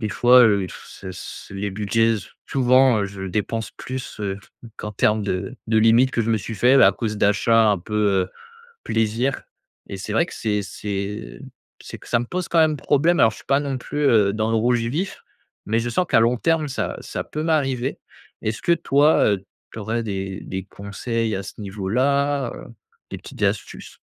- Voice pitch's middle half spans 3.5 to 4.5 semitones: Yes, average, 4.2 semitones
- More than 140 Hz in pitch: No, low, 115 Hz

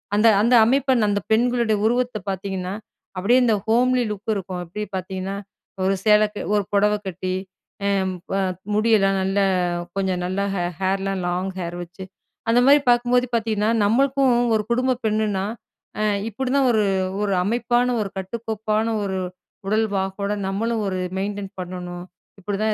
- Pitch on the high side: Yes, high, 210 Hz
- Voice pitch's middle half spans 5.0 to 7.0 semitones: No, average, 3.2 semitones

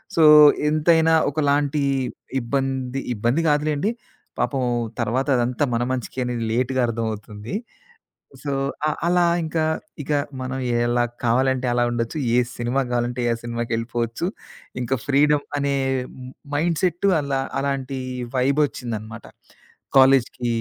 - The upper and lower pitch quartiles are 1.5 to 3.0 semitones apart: No, average, 3.4 semitones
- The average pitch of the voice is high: No, low, 130 Hz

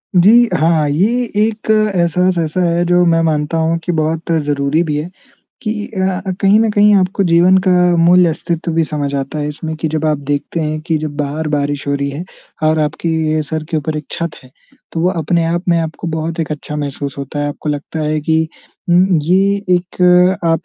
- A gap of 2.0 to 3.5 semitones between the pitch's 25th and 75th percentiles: Yes, average, 2.8 semitones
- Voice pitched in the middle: Yes, medium, 160 Hz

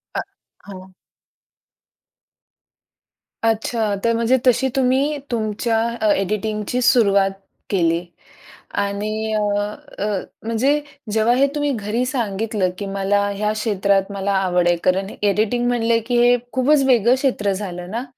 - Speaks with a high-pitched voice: Yes, high, 215 Hz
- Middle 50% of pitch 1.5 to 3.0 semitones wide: No, average, 3.5 semitones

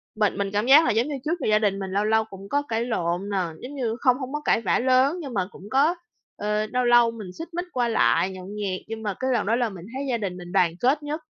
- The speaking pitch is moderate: No, high, 225 Hz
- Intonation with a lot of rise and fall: No, average, 4.7 semitones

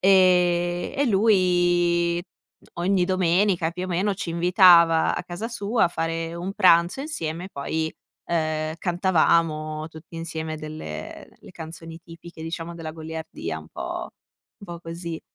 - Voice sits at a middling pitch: Yes, medium, 170 Hz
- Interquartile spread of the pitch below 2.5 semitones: Yes, narrow, 2.0 semitones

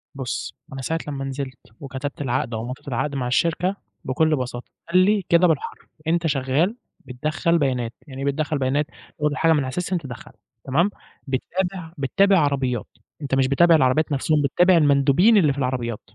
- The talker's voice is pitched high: No, medium, 140 Hz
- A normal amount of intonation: Yes, average, 3.9 semitones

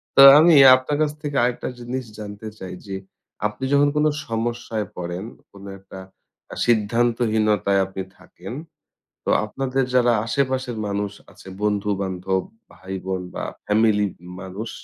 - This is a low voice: Yes, low, 105 Hz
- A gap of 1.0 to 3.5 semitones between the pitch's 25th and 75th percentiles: No, average, 4.0 semitones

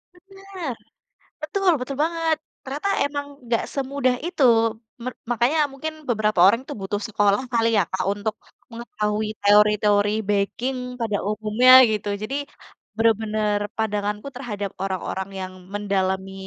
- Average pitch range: Yes, average, 4.8 semitones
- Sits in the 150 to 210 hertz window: No, high, 220 Hz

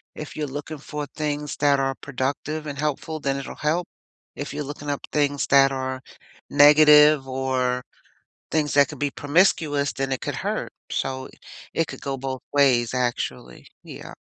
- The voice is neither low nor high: Yes, medium, 145 Hz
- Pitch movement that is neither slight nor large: No, narrow, 1.9 semitones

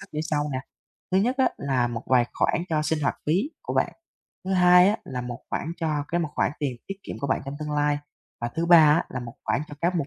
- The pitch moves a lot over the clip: No, average, 4.5 semitones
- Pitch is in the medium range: Yes, medium, 150 Hz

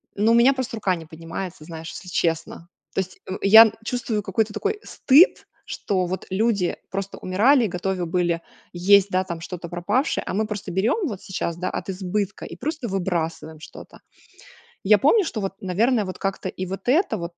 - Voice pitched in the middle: No, high, 195 Hz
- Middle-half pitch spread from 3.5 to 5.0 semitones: Yes, average, 3.8 semitones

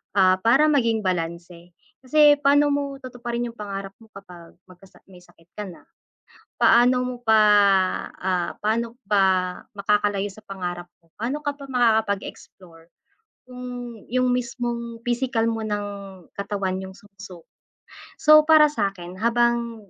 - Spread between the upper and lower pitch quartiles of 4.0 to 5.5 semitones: Yes, average, 4.7 semitones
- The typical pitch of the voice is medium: No, high, 220 Hz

